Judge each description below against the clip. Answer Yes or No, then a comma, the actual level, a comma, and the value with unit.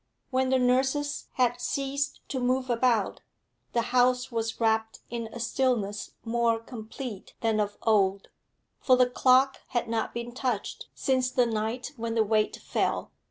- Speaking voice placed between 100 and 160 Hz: No, high, 240 Hz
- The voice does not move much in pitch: Yes, narrow, 2.3 semitones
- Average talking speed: Yes, average, 155 wpm